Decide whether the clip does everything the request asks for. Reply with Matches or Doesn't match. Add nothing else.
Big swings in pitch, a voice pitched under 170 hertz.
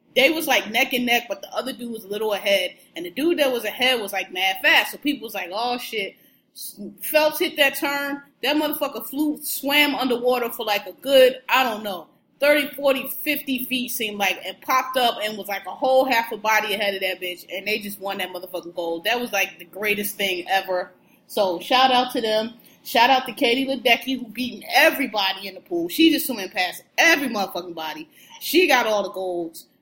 Doesn't match